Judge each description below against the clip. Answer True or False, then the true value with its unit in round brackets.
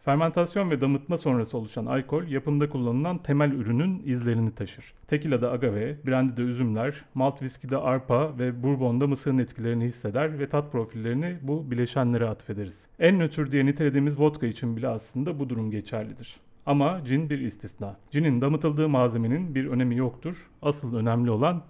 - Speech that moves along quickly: True (150 wpm)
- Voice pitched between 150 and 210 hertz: False (130 Hz)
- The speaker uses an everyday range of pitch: True (3.8 semitones)